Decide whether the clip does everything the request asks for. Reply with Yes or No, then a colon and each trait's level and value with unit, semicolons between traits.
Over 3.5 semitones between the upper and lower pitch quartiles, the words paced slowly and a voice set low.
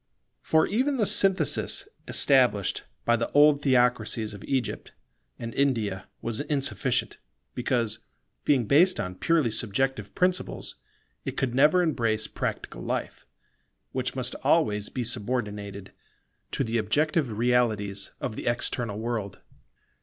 Yes: average, 4.7 semitones; slow, 125 wpm; low, 120 Hz